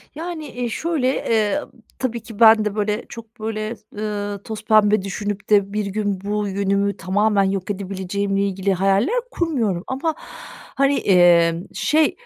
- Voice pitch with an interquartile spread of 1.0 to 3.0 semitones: Yes, narrow, 2.4 semitones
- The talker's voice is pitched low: No, high, 210 Hz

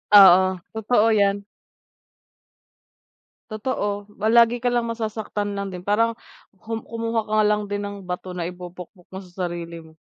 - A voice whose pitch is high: Yes, high, 205 Hz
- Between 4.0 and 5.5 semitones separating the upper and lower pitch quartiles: No, average, 3.5 semitones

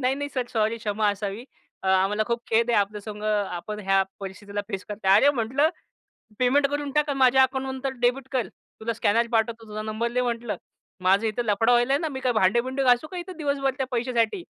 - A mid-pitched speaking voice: No, high, 235 Hz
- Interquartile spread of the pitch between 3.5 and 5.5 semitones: Yes, average, 4.0 semitones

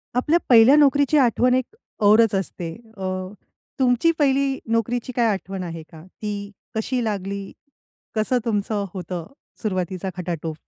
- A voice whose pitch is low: No, high, 215 Hz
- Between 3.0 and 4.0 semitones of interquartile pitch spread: No, average, 4.9 semitones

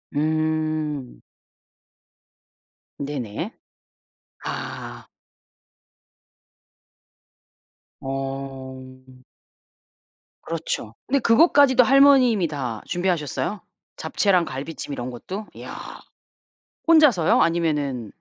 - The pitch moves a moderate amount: No, wide, 6.7 semitones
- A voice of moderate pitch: Yes, medium, 155 Hz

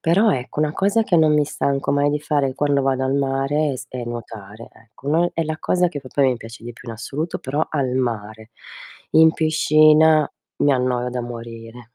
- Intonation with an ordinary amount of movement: Yes, average, 4.1 semitones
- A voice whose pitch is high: No, low, 135 Hz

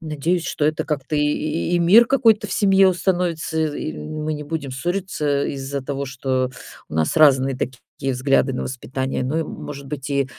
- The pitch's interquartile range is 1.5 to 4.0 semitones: Yes, average, 3.6 semitones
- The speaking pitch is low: No, medium, 145 Hz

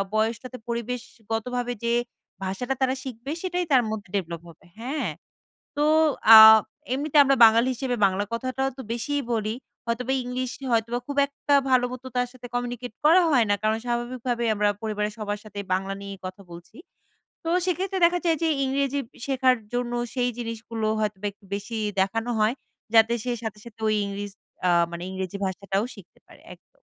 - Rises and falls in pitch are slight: No, average, 3.5 semitones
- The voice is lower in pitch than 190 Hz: No, high, 235 Hz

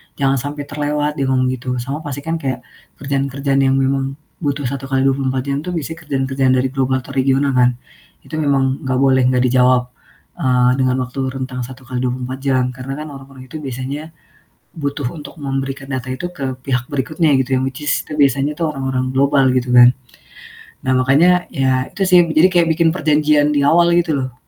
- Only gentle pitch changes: Yes, narrow, 2.0 semitones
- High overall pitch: No, low, 135 Hz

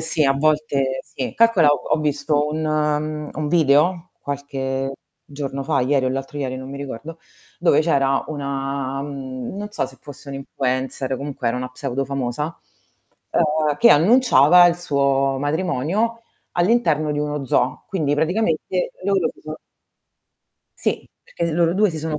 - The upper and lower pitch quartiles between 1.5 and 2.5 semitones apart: No, average, 2.9 semitones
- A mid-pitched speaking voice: Yes, medium, 145 Hz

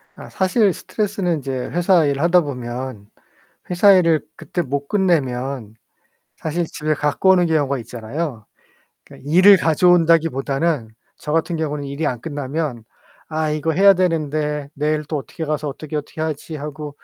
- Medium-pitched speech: Yes, medium, 155 Hz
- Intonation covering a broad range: No, average, 3.3 semitones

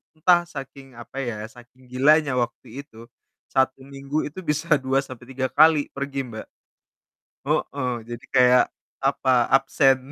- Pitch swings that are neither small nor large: No, narrow, 2.3 semitones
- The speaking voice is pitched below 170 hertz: Yes, low, 135 Hz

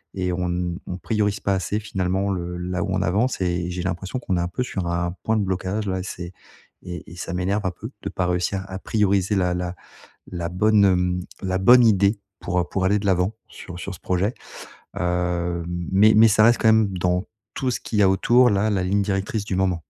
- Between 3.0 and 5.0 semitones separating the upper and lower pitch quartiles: No, narrow, 2.4 semitones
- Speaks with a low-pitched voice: Yes, very low, 95 Hz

